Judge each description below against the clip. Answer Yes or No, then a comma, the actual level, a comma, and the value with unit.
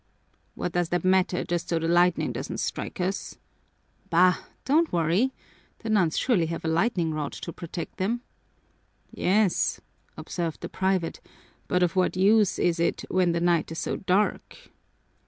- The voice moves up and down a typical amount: No, narrow, 2.3 semitones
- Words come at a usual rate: Yes, average, 155 wpm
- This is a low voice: No, medium, 180 Hz